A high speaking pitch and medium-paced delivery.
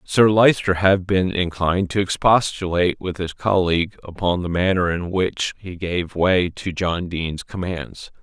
No: very low, 90 Hz; average, 160 wpm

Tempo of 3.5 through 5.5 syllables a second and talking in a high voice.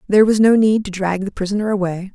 No: 6.5 syllables/s; high, 200 Hz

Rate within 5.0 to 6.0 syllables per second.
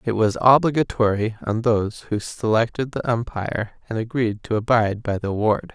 Yes: 5.5 syllables/s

